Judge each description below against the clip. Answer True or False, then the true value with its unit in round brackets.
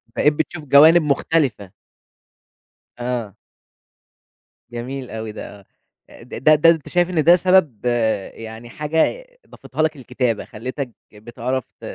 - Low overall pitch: True (130 Hz)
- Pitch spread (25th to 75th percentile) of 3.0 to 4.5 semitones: False (5.4 semitones)